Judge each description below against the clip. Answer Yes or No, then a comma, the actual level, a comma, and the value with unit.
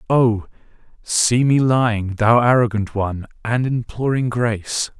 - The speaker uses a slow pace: Yes, slow, 120 wpm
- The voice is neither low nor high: No, low, 115 Hz